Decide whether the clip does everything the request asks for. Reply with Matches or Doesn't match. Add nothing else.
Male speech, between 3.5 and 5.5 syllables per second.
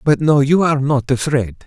Matches